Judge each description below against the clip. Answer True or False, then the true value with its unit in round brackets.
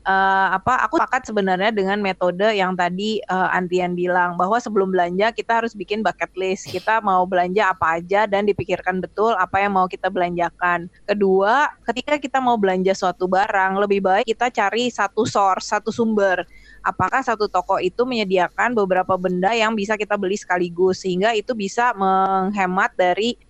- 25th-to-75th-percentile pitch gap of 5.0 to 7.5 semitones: False (3.0 semitones)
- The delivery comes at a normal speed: False (165 wpm)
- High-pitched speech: True (195 Hz)